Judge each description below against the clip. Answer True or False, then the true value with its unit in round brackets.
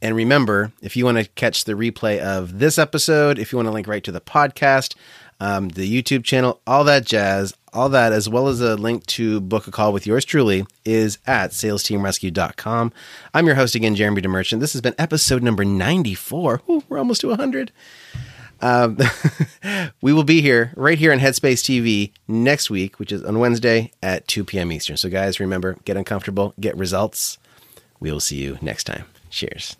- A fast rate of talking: False (195 wpm)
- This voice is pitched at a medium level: False (115 Hz)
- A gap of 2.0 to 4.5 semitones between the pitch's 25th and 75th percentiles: False (5.1 semitones)